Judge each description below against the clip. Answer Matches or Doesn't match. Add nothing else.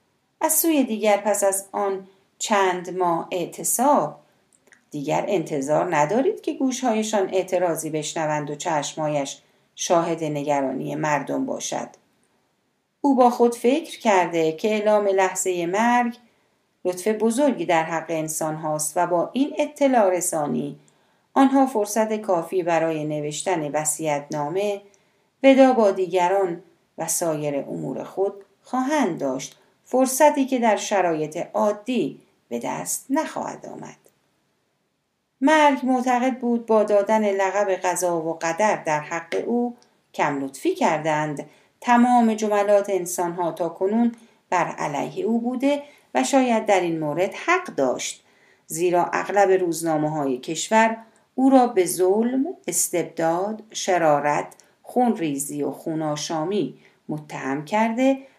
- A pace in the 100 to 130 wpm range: Matches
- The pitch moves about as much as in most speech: Doesn't match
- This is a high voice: Matches